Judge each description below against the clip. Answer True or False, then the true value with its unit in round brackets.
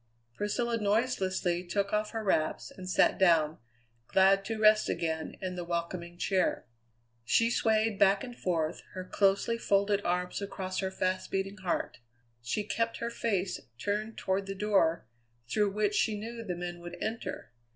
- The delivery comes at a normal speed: True (160 wpm)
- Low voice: False (195 Hz)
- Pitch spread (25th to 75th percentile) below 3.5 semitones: True (3.0 semitones)